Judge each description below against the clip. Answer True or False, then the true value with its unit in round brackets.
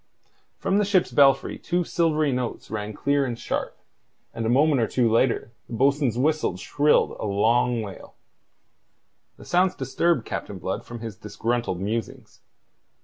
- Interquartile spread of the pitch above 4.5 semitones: True (4.9 semitones)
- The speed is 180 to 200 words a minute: False (150 wpm)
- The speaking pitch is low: True (125 Hz)